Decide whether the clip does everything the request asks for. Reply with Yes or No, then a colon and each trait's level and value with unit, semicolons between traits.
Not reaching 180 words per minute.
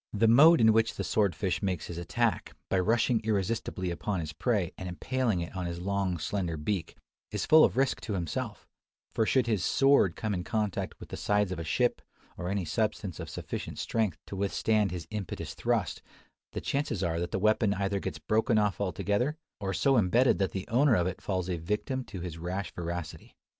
No: fast, 205 wpm